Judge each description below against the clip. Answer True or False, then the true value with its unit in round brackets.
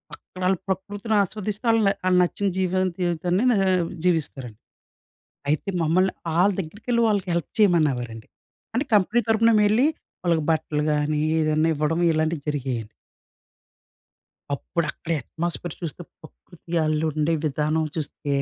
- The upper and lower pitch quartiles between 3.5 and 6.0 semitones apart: True (4.1 semitones)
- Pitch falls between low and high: True (170 Hz)